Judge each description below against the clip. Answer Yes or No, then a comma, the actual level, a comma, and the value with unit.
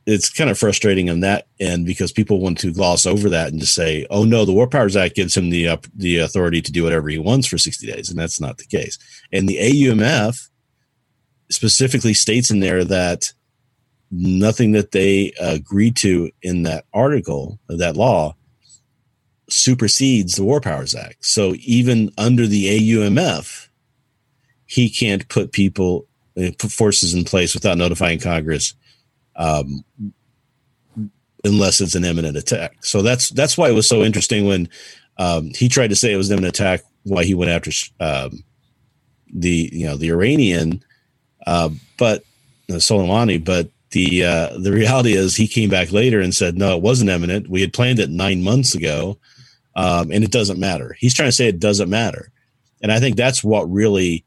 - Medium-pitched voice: No, low, 100 Hz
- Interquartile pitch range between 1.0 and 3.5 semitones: No, average, 5.3 semitones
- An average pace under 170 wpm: No, average, 180 wpm